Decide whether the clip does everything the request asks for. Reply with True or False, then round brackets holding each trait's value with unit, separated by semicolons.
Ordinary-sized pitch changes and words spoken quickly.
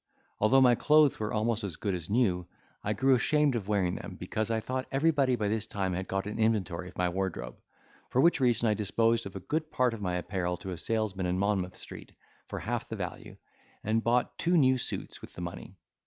True (4.8 semitones; 220 wpm)